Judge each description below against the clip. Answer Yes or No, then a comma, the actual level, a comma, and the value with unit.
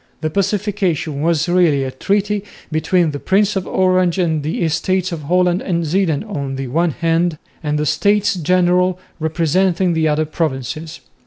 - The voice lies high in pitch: No, medium, 170 Hz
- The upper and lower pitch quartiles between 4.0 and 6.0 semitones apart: No, average, 3.1 semitones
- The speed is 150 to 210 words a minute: Yes, average, 160 wpm